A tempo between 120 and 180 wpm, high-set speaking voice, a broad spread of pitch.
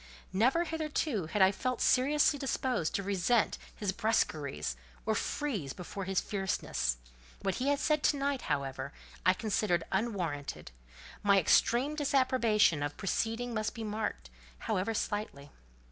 Yes: average, 140 wpm; high, 210 Hz; wide, 6.3 semitones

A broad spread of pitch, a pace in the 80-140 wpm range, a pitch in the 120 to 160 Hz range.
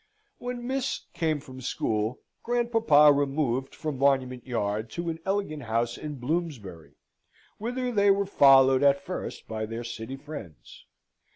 Yes: wide, 7.0 semitones; slow, 135 wpm; medium, 140 Hz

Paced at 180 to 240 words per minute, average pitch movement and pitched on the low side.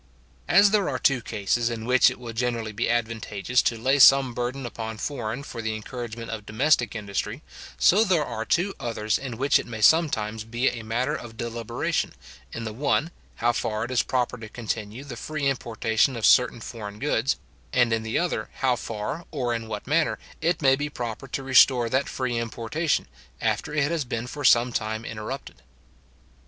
Yes: average, 190 wpm; average, 3.3 semitones; low, 120 Hz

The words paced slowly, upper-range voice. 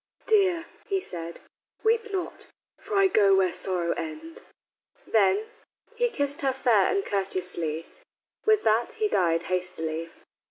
Yes: slow, 130 wpm; high, 220 Hz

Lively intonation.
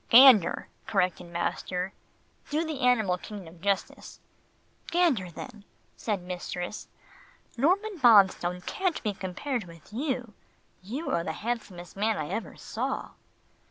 Yes: wide, 6.3 semitones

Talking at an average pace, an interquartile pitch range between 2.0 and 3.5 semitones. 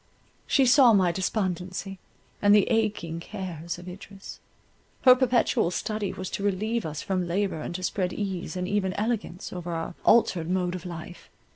Yes: average, 165 wpm; average, 2.9 semitones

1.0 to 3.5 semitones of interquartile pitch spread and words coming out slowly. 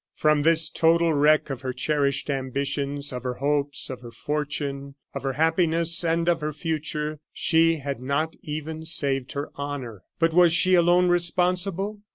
No: average, 2.9 semitones; average, 165 wpm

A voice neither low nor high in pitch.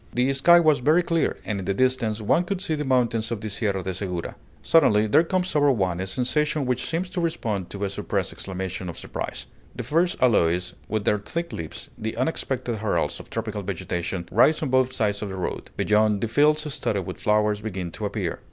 No: low, 110 Hz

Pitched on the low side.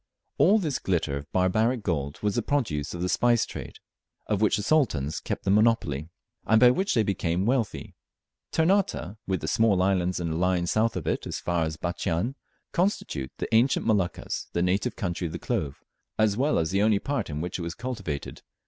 Yes: very low, 95 Hz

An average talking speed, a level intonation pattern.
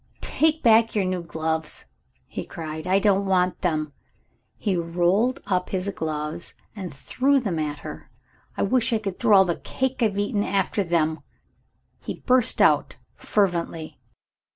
No: average, 150 wpm; average, 4.5 semitones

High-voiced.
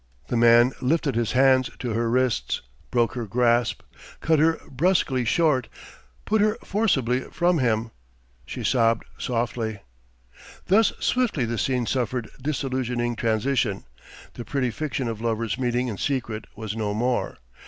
No: low, 125 Hz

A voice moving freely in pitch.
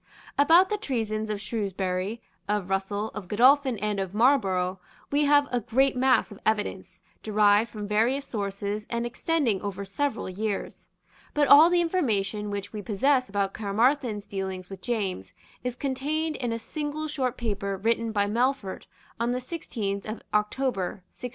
No: average, 4.8 semitones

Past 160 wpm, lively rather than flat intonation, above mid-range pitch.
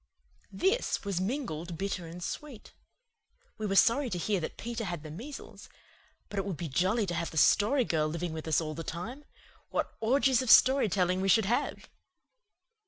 Yes: average, 185 wpm; wide, 5.9 semitones; high, 195 Hz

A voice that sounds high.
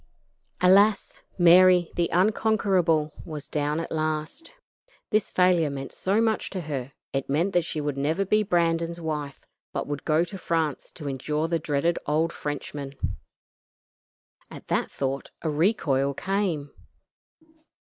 No: medium, 165 Hz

